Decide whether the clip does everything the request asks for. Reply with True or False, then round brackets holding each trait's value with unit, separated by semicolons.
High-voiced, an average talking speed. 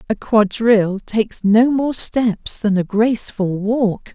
True (220 Hz; 145 wpm)